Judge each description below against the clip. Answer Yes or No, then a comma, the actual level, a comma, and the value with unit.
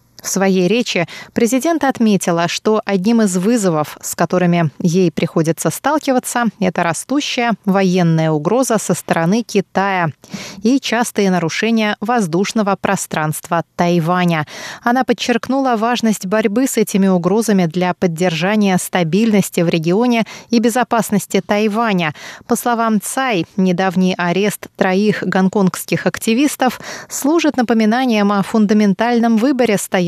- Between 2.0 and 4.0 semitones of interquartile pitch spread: No, average, 4.4 semitones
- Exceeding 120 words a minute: No, slow, 110 wpm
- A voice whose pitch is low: No, high, 200 Hz